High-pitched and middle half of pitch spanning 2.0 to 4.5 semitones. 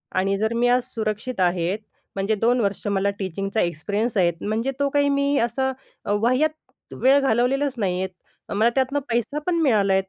No: high, 230 Hz; average, 5.1 semitones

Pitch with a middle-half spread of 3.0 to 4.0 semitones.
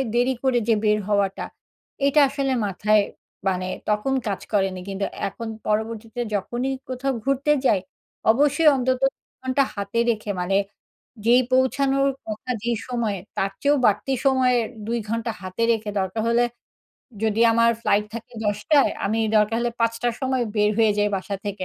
Yes: average, 3.7 semitones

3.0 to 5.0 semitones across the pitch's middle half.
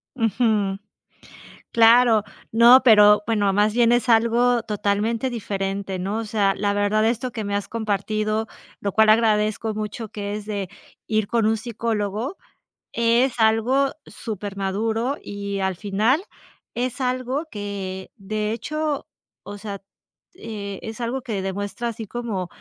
No: narrow, 2.4 semitones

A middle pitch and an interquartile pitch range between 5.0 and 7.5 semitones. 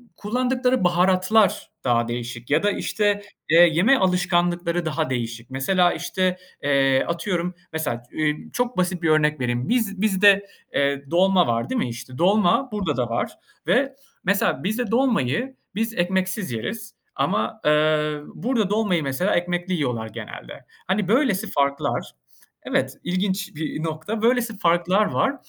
Yes: medium, 180 Hz; wide, 5.6 semitones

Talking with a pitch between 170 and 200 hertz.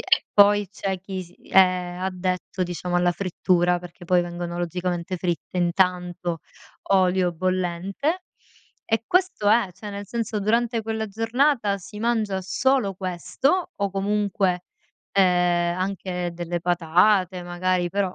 Yes: medium, 185 Hz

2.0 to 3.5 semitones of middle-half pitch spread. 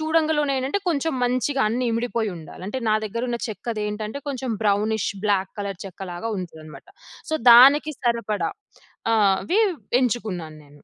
No: average, 5.0 semitones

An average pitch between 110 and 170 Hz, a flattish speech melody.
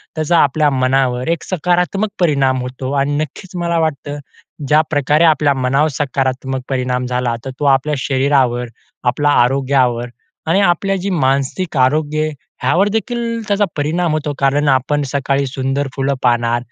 No: medium, 140 Hz; average, 3.2 semitones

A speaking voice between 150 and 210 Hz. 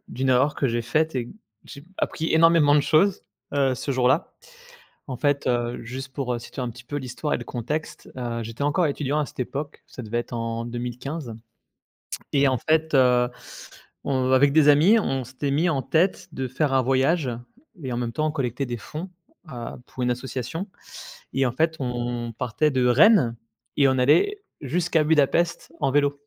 No: low, 135 Hz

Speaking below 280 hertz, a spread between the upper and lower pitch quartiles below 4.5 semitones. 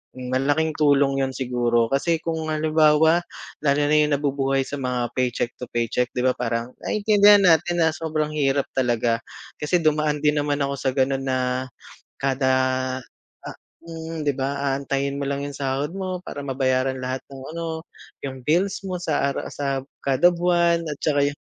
Yes: medium, 140 Hz; average, 3.2 semitones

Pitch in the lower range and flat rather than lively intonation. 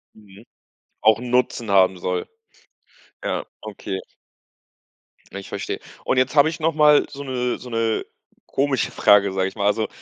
No: low, 115 Hz; average, 4.9 semitones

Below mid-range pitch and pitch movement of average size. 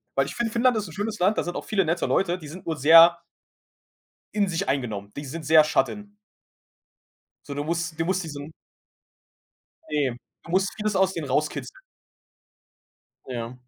No: medium, 170 Hz; average, 4.5 semitones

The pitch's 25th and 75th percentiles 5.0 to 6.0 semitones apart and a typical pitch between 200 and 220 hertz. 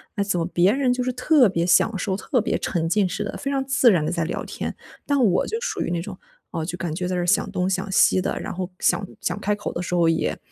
No: wide, 5.5 semitones; high, 190 Hz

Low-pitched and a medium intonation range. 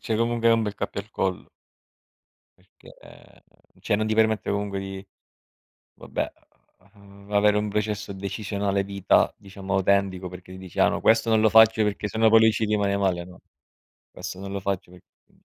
No: low, 100 Hz; narrow, 2.0 semitones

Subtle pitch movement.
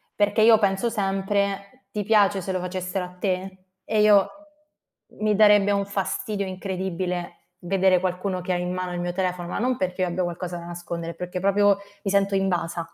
Yes: narrow, 1.9 semitones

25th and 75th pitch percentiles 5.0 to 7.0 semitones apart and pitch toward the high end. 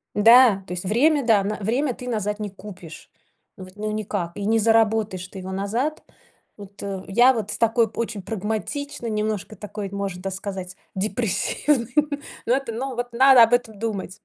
No: average, 3.0 semitones; high, 215 Hz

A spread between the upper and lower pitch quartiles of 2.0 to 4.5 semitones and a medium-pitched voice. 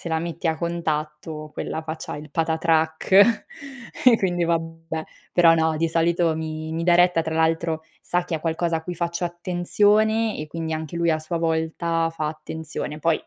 No: narrow, 1.4 semitones; medium, 165 Hz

